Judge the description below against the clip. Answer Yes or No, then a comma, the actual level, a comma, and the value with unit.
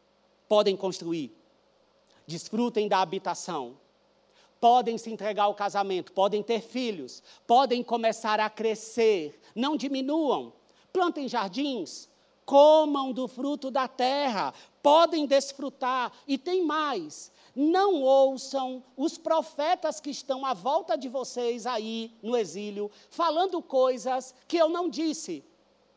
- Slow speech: Yes, slow, 115 wpm